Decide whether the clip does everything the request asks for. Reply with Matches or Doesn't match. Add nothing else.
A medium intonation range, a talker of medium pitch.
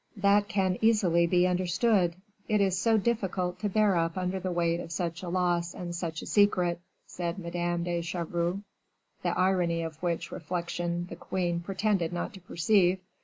Doesn't match